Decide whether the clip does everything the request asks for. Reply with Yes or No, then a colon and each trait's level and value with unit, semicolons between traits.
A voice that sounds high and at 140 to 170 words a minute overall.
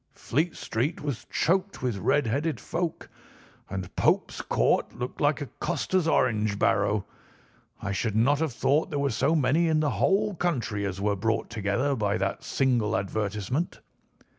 No: low, 125 Hz; average, 160 wpm